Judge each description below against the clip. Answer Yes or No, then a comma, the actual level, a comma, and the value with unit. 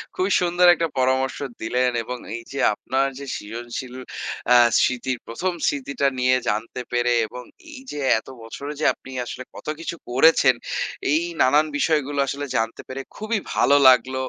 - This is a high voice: No, low, 130 Hz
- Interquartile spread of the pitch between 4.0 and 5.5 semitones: No, average, 2.9 semitones